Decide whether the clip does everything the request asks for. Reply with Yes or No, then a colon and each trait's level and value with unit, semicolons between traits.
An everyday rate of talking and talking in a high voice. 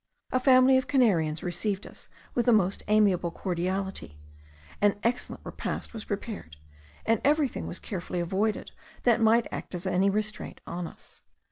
Yes: average, 150 wpm; high, 205 Hz